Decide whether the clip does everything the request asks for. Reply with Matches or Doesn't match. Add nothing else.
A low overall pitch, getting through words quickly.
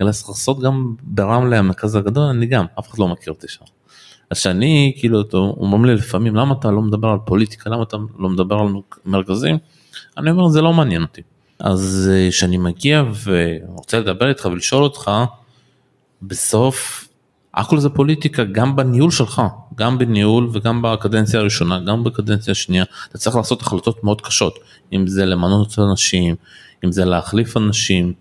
Matches